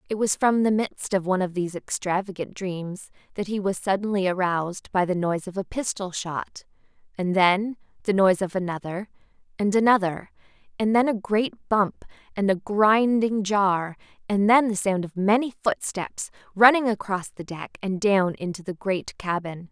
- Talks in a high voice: Yes, high, 195 Hz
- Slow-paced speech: No, average, 175 wpm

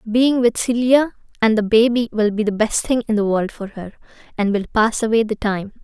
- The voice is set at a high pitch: Yes, high, 220 Hz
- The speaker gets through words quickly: Yes, fast, 225 wpm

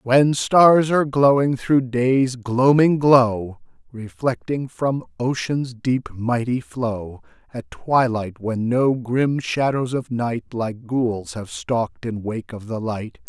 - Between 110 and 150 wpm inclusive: Yes, average, 140 wpm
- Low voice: Yes, low, 125 Hz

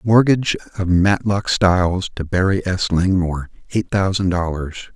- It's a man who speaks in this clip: Yes, male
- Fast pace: No, slow, 135 wpm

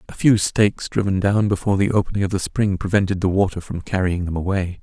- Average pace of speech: No, fast, 225 wpm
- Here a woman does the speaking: No, male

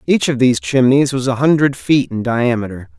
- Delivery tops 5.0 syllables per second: Yes, 5.4 syllables/s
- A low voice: Yes, low, 125 Hz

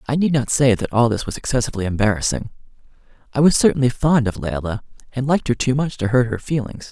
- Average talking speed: No, fast, 215 wpm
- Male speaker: Yes, male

